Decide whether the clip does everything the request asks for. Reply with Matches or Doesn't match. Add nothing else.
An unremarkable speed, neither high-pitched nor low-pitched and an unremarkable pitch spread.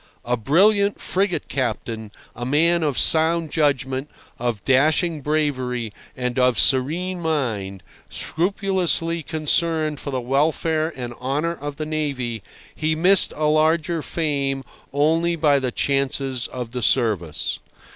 Doesn't match